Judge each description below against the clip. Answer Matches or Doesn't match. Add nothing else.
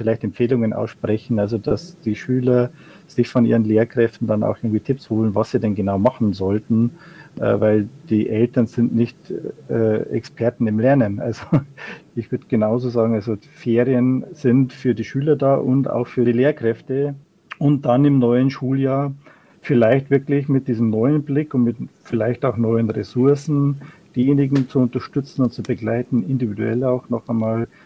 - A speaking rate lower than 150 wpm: Doesn't match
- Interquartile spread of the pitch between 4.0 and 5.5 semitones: Doesn't match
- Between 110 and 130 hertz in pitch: Matches